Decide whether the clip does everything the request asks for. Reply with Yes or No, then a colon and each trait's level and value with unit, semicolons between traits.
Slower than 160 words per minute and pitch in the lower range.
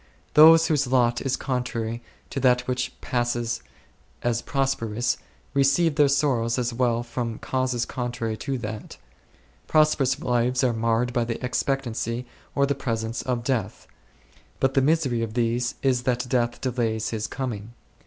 Yes: average, 150 wpm; low, 125 Hz